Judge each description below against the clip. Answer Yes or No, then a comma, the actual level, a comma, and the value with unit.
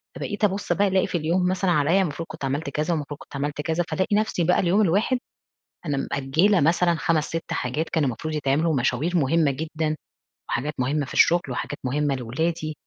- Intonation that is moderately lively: Yes, average, 3.5 semitones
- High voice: No, medium, 160 Hz